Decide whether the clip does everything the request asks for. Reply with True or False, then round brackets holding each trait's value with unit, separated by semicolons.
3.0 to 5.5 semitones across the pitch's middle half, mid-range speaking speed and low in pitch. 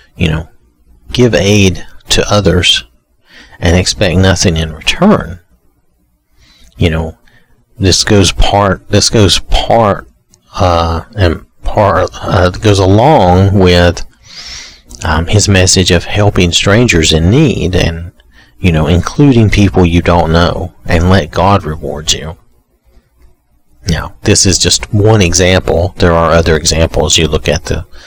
False (3.7 semitones; 130 wpm; 85 Hz)